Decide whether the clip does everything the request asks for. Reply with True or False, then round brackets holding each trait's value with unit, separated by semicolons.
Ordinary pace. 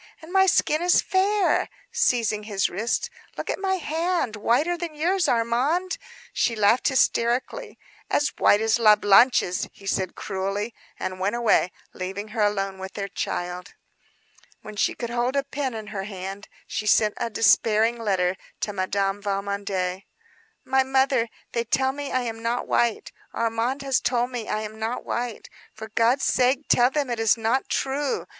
True (165 wpm)